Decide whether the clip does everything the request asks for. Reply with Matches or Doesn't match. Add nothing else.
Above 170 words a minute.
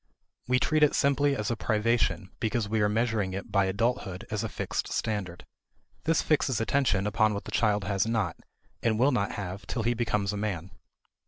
Matches